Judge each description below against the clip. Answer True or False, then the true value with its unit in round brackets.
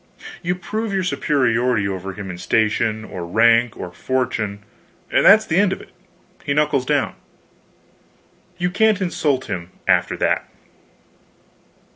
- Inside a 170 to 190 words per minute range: False (135 wpm)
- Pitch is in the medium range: False (125 Hz)